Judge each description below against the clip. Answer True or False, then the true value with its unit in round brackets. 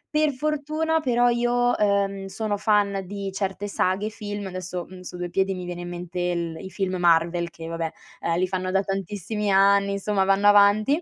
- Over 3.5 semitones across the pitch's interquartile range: False (2.5 semitones)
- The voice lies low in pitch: False (195 Hz)